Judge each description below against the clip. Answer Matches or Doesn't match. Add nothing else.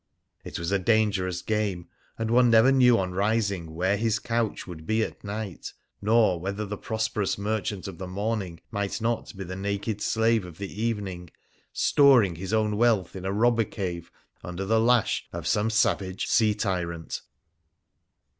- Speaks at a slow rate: Doesn't match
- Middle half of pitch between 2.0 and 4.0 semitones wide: Matches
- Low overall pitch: Matches